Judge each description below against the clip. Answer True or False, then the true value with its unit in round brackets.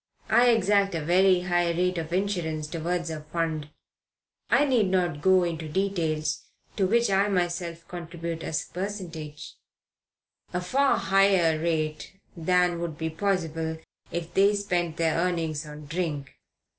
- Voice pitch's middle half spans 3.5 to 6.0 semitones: False (2.9 semitones)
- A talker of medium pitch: True (175 Hz)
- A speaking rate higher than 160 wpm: False (140 wpm)